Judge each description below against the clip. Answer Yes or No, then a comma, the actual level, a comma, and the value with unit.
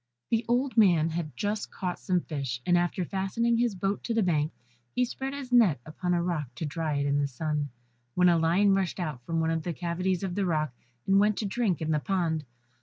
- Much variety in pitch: No, average, 4.2 semitones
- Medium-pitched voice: Yes, medium, 175 Hz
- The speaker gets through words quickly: Yes, fast, 235 wpm